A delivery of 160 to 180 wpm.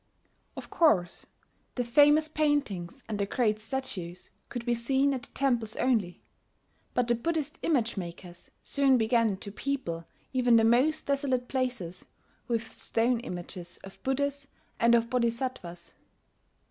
No: slow, 135 wpm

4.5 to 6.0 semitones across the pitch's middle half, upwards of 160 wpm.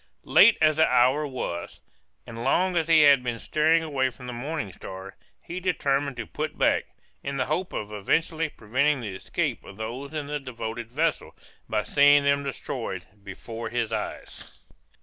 Yes: average, 4.9 semitones; average, 170 wpm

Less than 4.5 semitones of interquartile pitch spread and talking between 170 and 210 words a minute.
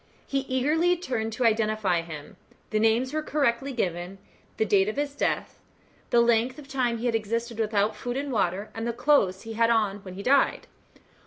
Yes: average, 3.6 semitones; average, 190 wpm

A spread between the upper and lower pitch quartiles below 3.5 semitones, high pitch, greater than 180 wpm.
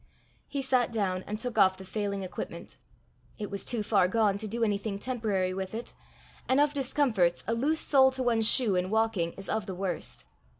No: average, 4.0 semitones; high, 215 Hz; average, 200 wpm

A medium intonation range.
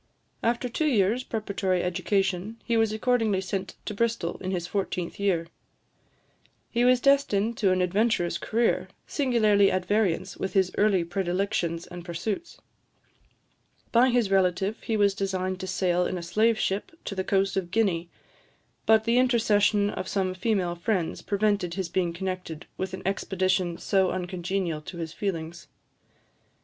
Yes: average, 3.1 semitones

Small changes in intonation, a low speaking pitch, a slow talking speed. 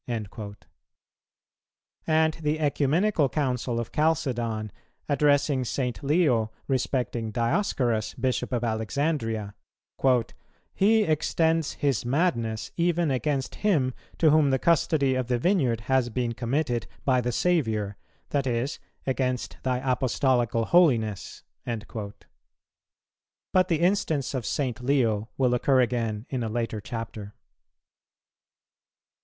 No: average, 4.4 semitones; low, 130 Hz; slow, 110 wpm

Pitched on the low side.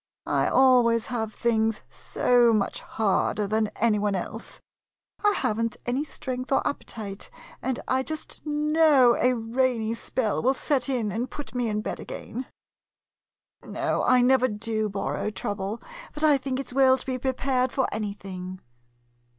No: high, 245 Hz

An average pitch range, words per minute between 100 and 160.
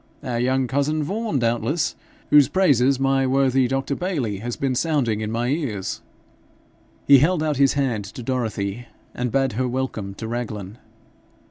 Yes: average, 3.2 semitones; average, 155 wpm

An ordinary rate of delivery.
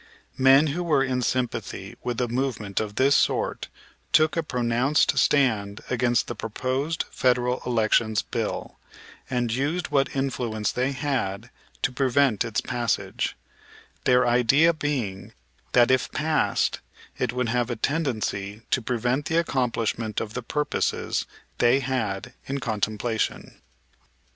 No: slow, 130 wpm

